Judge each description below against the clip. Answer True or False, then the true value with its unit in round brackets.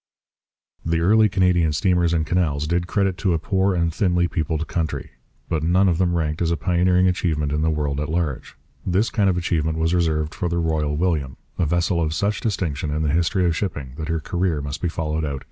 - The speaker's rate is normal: False (225 wpm)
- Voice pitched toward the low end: True (85 Hz)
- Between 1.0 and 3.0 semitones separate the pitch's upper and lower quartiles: True (2.6 semitones)